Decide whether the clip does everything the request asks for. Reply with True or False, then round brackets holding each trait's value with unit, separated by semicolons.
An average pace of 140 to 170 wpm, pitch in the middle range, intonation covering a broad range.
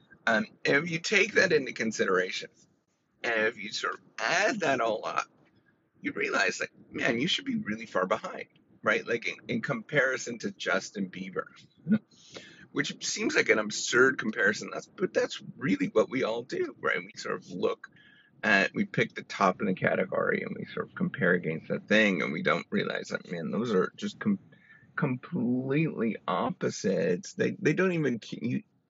False (180 wpm; 175 Hz; 8.0 semitones)